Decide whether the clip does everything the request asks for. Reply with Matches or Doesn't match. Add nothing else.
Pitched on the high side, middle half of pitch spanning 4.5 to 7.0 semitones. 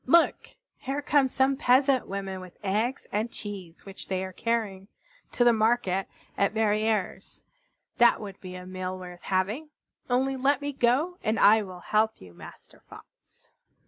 Matches